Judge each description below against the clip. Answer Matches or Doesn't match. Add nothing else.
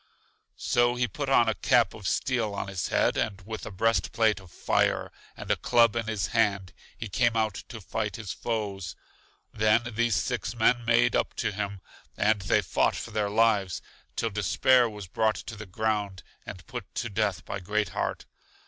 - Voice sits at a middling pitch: Doesn't match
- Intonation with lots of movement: Doesn't match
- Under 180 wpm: Doesn't match